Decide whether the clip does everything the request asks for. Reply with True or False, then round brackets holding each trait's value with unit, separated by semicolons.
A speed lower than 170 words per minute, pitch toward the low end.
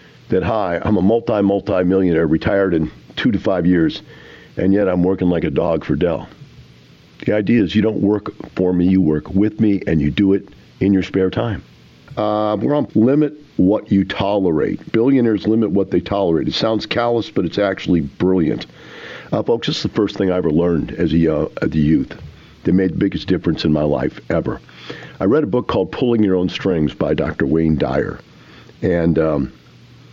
False (195 wpm; 95 Hz)